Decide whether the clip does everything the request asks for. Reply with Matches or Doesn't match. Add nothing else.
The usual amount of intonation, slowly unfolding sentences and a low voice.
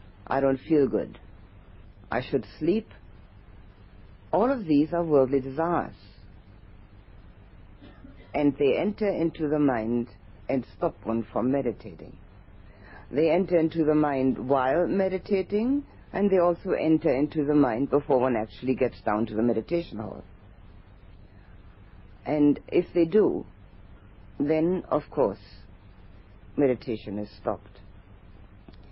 Doesn't match